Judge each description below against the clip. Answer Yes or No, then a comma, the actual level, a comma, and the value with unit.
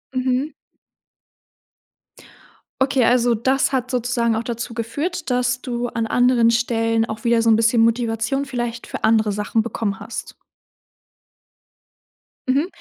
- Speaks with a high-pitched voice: Yes, high, 235 Hz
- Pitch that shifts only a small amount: Yes, narrow, 1.9 semitones